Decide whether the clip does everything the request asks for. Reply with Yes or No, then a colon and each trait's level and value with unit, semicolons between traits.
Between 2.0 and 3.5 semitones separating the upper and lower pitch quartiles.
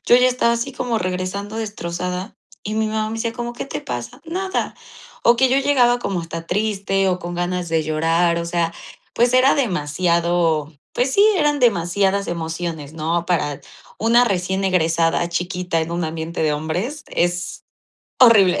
No: wide, 5.6 semitones